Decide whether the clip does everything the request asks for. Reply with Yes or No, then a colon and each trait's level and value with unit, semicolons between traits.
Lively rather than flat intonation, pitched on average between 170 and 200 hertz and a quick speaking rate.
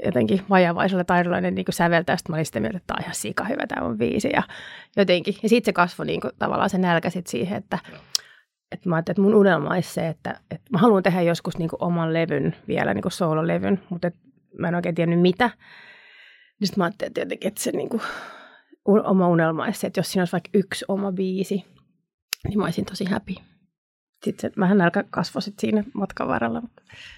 No: average, 2.8 semitones; high, 190 Hz; fast, 215 wpm